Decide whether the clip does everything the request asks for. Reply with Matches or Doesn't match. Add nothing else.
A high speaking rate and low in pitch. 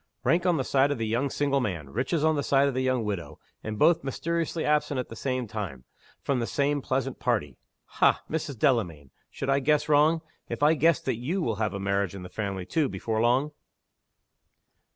Matches